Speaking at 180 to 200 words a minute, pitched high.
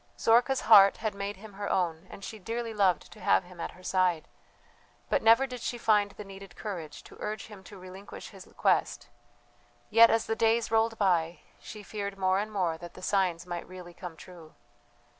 Yes: average, 195 wpm; high, 200 Hz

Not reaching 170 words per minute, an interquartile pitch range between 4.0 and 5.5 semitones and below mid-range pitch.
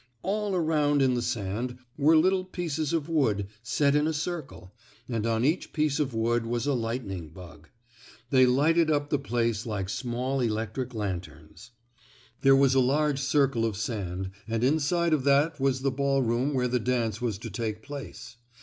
No: average, 175 wpm; average, 4.4 semitones; low, 130 Hz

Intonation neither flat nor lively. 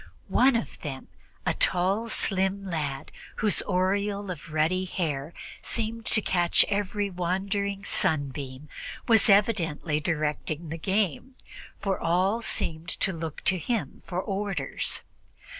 Yes: average, 4.1 semitones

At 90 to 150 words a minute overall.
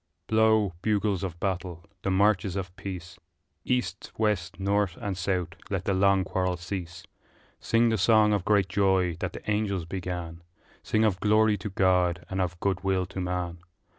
No: average, 165 wpm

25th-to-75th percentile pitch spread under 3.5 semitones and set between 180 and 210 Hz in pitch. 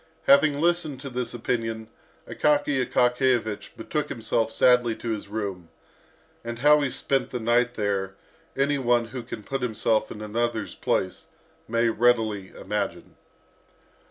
No: average, 3.0 semitones; low, 120 Hz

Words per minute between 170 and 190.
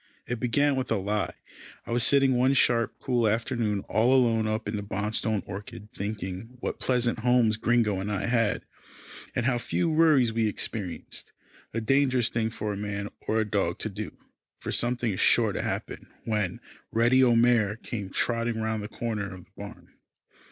Yes: average, 175 wpm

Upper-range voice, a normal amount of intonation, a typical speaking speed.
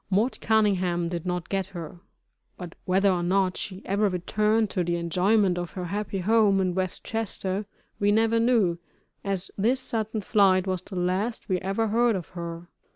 Yes: high, 195 Hz; average, 3.0 semitones; average, 175 wpm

